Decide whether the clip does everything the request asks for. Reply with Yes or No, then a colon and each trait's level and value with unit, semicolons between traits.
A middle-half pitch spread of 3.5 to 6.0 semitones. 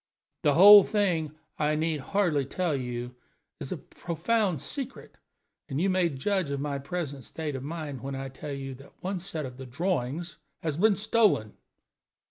Yes: average, 5.2 semitones